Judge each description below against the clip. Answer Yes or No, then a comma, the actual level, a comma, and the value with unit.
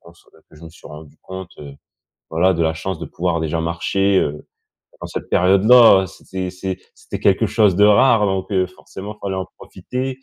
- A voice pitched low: Yes, very low, 95 Hz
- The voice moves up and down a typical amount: Yes, average, 3.1 semitones